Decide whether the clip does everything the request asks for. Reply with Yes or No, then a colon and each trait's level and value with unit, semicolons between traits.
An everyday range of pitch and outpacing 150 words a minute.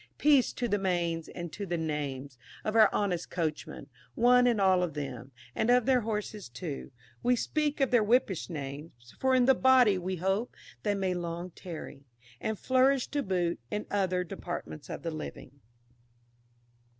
No: wide, 6.7 semitones; average, 170 wpm